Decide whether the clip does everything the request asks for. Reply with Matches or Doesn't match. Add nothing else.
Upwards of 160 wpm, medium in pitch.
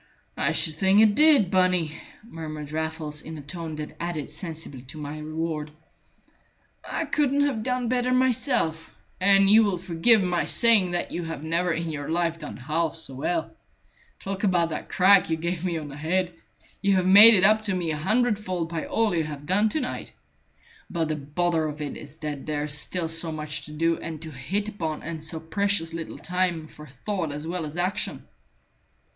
Matches